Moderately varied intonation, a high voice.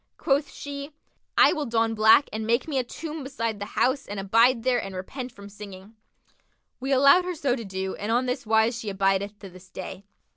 Yes: average, 4.9 semitones; high, 230 Hz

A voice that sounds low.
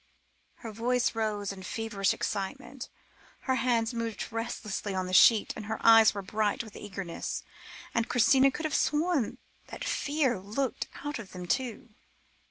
No: high, 225 Hz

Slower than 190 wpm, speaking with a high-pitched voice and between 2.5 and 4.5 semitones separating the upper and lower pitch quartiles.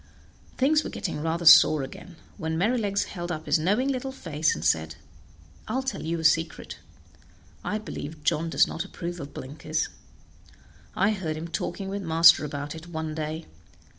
No: average, 165 wpm; medium, 165 Hz; average, 4.0 semitones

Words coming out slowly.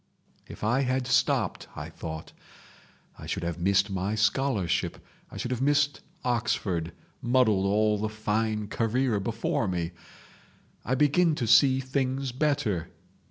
Yes: slow, 130 wpm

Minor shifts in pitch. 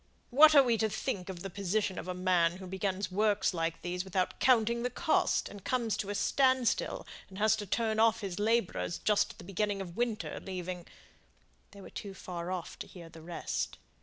No: average, 3.4 semitones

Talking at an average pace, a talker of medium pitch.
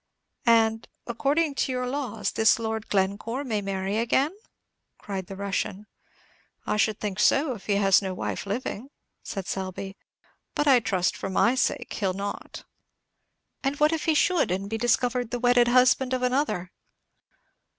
No: average, 160 wpm; high, 225 Hz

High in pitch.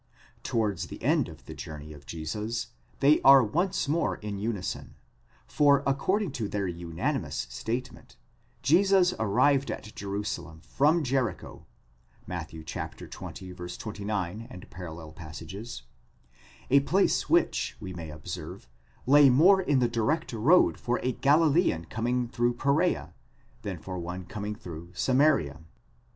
No: low, 110 Hz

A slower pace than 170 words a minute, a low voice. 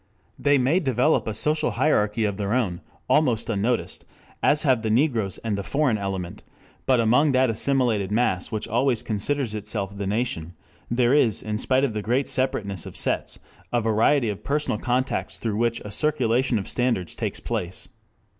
No: average, 175 wpm; low, 115 Hz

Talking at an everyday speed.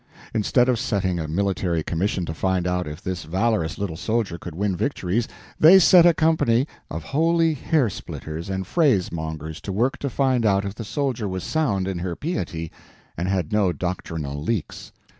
Yes: average, 180 wpm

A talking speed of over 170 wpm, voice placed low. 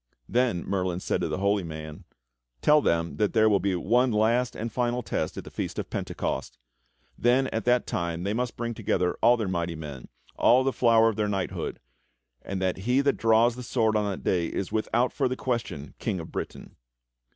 Yes: average, 200 wpm; low, 110 Hz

